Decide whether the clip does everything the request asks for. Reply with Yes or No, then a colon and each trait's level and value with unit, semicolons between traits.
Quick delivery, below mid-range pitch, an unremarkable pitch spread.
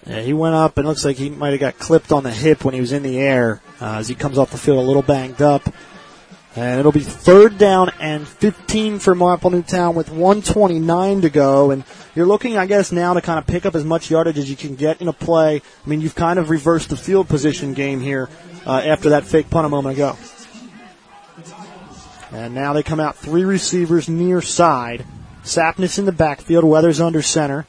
No: fast, 225 wpm; medium, 160 Hz; average, 3.9 semitones